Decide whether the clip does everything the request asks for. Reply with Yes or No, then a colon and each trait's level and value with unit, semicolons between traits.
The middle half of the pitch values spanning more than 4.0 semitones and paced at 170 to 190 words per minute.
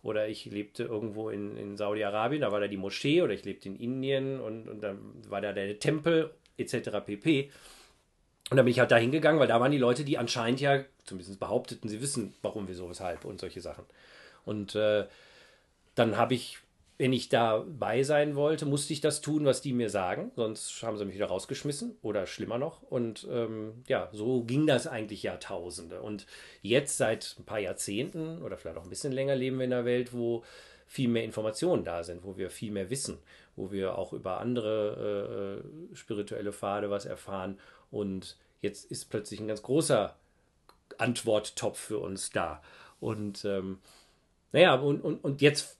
Yes: average, 4.7 semitones; average, 185 wpm